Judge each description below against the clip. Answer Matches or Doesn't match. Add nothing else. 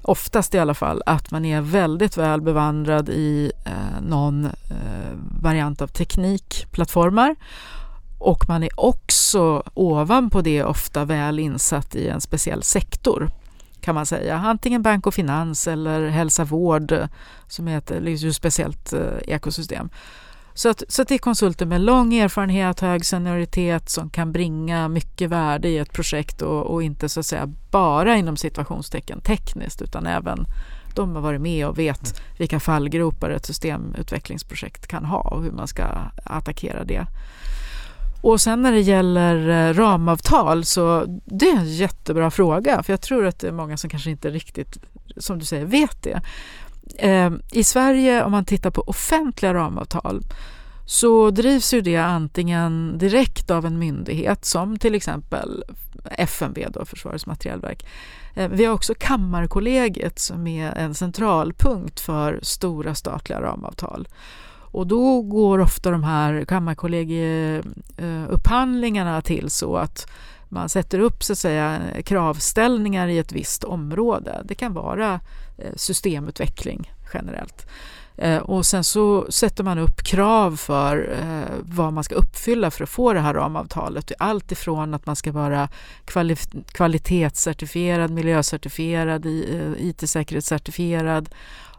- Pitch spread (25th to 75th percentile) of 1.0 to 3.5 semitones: Doesn't match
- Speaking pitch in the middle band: Matches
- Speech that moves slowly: Doesn't match